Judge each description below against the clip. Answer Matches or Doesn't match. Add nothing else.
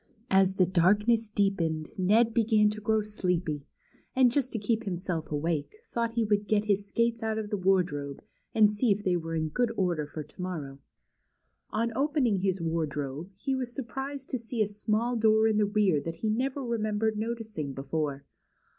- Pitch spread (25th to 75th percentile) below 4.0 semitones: Doesn't match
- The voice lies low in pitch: Doesn't match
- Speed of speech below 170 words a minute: Doesn't match